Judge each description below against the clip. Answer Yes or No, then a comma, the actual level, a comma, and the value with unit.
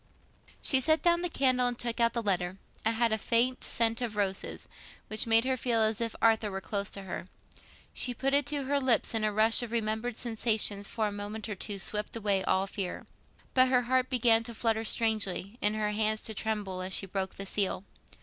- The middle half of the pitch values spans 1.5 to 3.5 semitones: Yes, average, 2.8 semitones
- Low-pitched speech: No, high, 220 Hz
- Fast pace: Yes, fast, 215 wpm